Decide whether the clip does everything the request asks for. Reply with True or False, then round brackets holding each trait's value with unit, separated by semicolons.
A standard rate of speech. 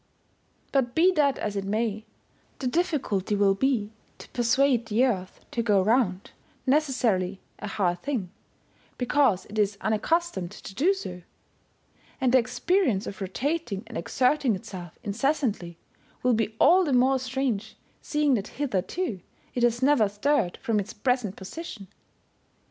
True (145 wpm)